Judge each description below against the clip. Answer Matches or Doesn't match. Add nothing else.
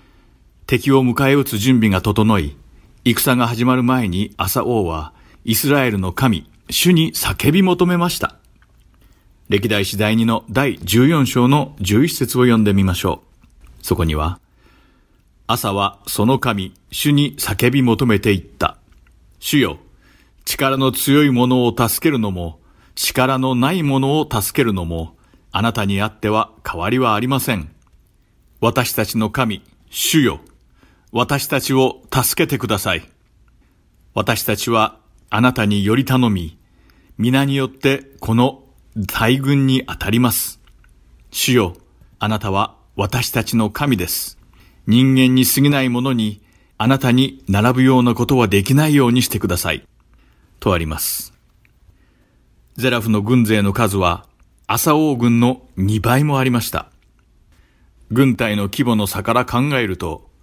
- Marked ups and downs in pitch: Doesn't match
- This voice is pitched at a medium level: Doesn't match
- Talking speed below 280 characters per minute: Matches